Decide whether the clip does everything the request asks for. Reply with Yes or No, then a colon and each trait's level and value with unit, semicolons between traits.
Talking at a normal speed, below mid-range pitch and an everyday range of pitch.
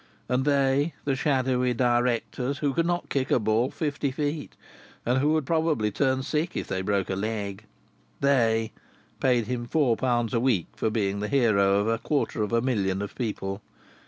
Yes: average, 185 wpm; low, 125 Hz; average, 4.4 semitones